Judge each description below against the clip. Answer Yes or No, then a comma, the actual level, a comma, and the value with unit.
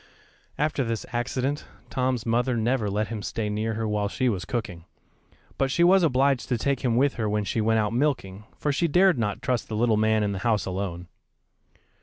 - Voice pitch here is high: No, low, 115 Hz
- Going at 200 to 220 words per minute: Yes, fast, 205 wpm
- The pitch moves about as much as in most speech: Yes, average, 3.7 semitones